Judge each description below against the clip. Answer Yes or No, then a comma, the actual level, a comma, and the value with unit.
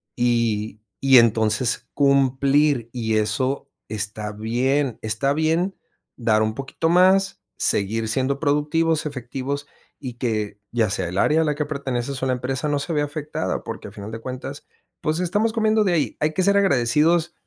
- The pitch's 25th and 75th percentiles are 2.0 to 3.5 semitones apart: No, average, 5.1 semitones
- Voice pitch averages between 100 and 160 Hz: Yes, low, 135 Hz